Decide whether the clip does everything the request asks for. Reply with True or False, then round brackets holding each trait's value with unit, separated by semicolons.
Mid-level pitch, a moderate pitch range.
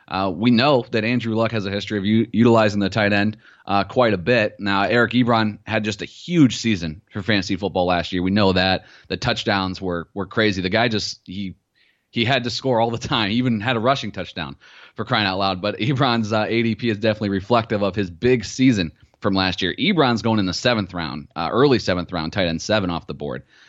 False (105 Hz; 3.5 semitones)